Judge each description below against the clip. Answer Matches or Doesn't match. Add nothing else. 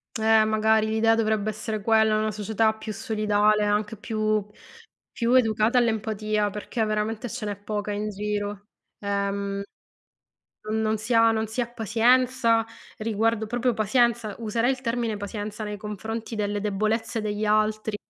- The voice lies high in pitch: Matches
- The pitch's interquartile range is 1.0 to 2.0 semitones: Matches